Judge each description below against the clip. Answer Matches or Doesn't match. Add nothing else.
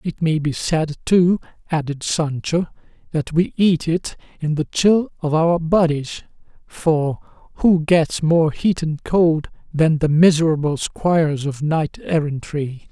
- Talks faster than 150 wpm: Doesn't match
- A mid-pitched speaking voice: Matches